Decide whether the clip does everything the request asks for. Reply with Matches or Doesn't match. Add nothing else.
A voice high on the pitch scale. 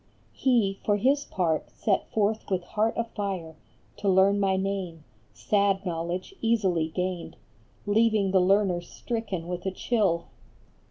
Matches